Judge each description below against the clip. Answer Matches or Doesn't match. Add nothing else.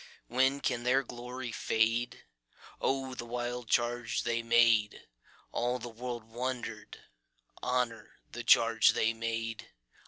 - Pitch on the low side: Matches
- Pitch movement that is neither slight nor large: Doesn't match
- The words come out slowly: Matches